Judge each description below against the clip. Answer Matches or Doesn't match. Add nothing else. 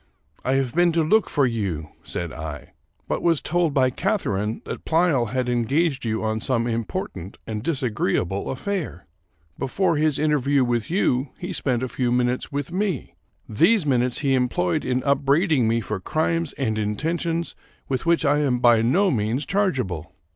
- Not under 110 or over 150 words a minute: Doesn't match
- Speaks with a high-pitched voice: Doesn't match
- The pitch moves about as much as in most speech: Doesn't match